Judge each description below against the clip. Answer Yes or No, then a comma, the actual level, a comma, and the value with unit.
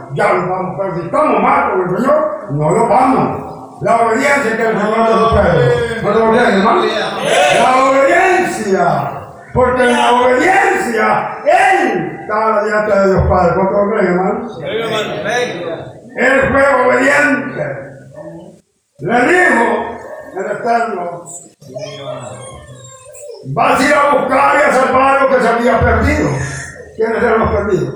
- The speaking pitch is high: Yes, high, 225 Hz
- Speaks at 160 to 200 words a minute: No, average, 135 wpm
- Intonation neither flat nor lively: No, wide, 6.6 semitones